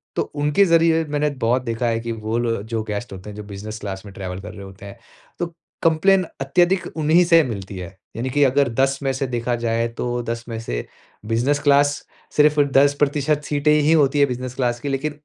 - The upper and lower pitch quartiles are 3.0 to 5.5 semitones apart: Yes, average, 4.5 semitones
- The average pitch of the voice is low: Yes, low, 125 Hz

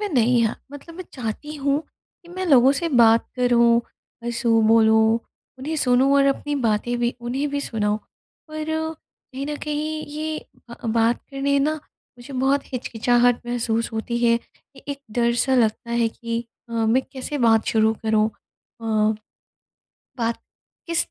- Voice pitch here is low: No, high, 240 Hz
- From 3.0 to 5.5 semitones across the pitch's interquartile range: Yes, average, 3.7 semitones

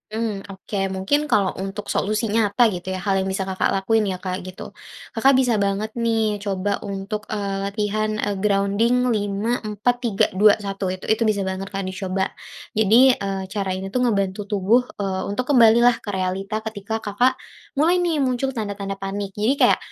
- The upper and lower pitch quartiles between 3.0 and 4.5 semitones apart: No, narrow, 2.6 semitones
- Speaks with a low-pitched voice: No, high, 205 Hz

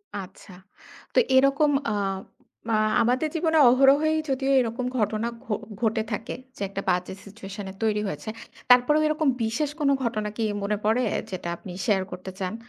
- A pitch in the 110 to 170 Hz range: No, high, 225 Hz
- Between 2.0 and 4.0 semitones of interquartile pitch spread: No, average, 5.2 semitones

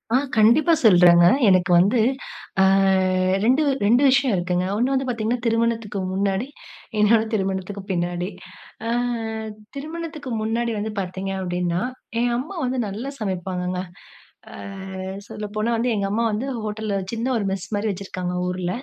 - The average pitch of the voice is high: Yes, high, 210 Hz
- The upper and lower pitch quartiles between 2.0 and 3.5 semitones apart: No, average, 4.2 semitones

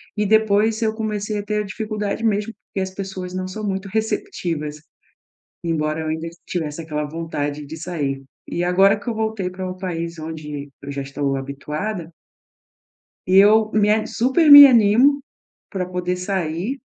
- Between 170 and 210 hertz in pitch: Yes, medium, 185 Hz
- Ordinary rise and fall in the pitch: Yes, average, 5.0 semitones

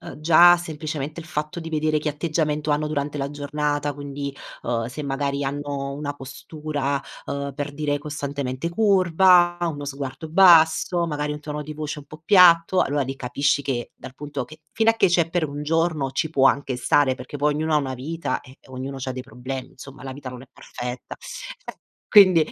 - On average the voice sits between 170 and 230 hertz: No, medium, 145 Hz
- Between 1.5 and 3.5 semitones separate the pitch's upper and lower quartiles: Yes, narrow, 2.4 semitones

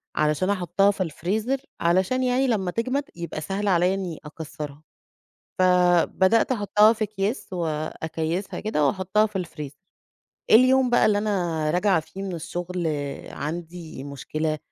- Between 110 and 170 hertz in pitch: No, medium, 185 Hz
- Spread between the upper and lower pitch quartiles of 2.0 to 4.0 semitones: No, average, 4.5 semitones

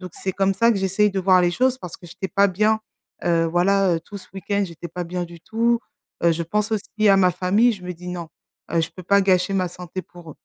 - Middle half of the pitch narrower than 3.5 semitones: Yes, narrow, 2.4 semitones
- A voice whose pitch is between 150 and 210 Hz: Yes, medium, 185 Hz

